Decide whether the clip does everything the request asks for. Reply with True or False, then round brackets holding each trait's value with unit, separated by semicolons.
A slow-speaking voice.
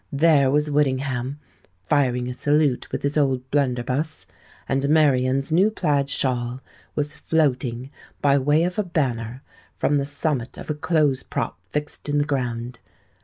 False (150 wpm)